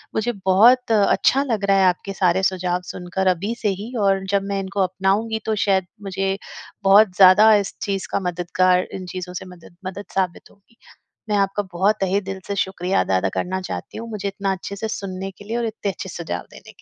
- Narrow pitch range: Yes, narrow, 1.7 semitones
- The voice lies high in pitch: Yes, high, 195 Hz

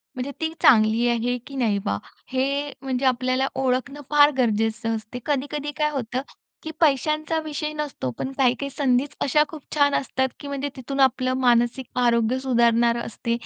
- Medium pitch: No, very high, 260 Hz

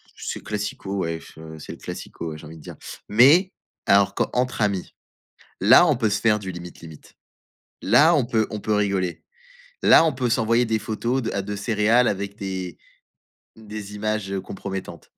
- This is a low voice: Yes, low, 105 Hz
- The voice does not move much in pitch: No, average, 3.1 semitones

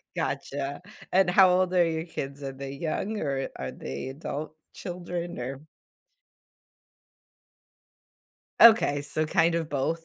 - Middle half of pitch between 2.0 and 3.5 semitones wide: No, average, 4.2 semitones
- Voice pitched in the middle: Yes, medium, 155 Hz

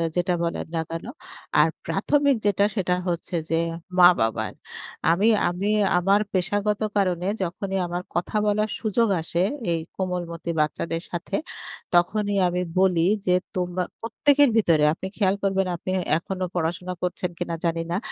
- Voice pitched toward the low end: No, medium, 180 Hz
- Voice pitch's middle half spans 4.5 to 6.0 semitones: No, average, 2.7 semitones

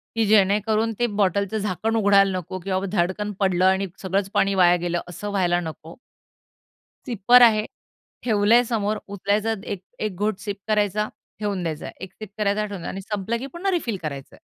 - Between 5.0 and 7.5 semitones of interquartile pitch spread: No, narrow, 2.4 semitones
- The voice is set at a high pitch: Yes, high, 200 Hz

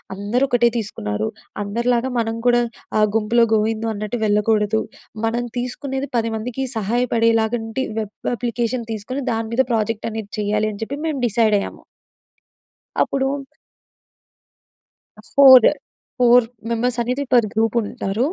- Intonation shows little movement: Yes, narrow, 2.3 semitones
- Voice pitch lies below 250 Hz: Yes, high, 225 Hz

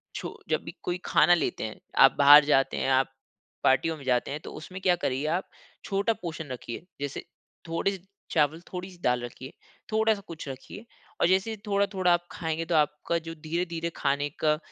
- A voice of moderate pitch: Yes, medium, 160 Hz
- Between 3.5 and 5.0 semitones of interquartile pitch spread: Yes, average, 4.2 semitones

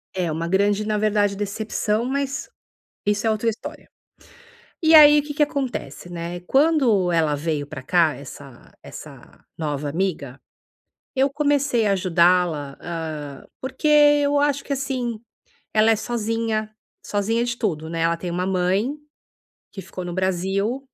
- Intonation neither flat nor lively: No, wide, 6.8 semitones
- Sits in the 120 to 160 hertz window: No, high, 205 Hz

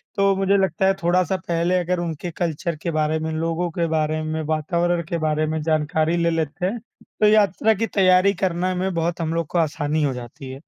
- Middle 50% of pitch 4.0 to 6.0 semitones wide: No, average, 2.7 semitones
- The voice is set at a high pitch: No, medium, 170 Hz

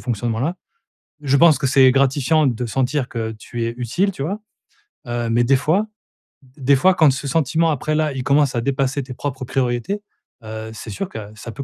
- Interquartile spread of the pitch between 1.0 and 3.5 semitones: No, average, 3.9 semitones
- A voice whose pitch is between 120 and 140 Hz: Yes, low, 135 Hz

